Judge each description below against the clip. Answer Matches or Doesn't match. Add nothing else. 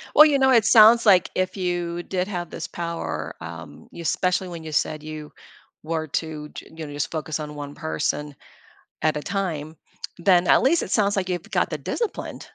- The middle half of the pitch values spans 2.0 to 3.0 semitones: Doesn't match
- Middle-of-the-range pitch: Matches